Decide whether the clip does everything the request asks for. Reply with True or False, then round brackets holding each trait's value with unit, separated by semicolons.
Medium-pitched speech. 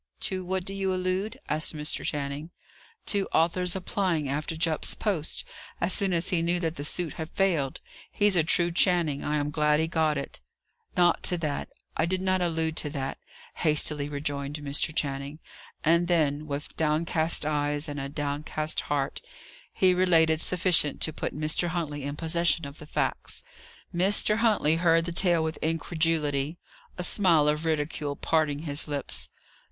True (160 Hz)